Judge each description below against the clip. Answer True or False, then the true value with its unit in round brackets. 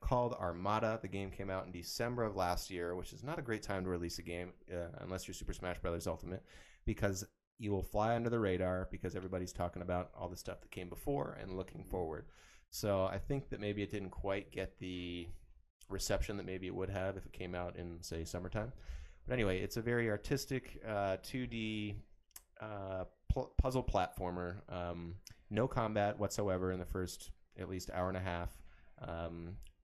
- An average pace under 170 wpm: False (195 wpm)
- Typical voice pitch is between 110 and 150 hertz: False (95 Hz)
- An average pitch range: True (3.1 semitones)